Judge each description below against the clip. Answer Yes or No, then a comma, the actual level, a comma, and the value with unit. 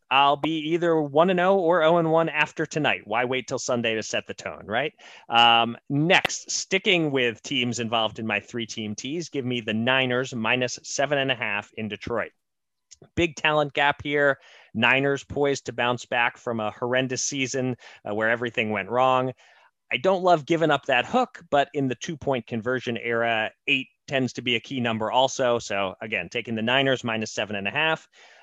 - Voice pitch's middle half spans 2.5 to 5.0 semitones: Yes, average, 3.9 semitones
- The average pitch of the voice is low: Yes, low, 130 Hz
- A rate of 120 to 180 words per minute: No, average, 195 wpm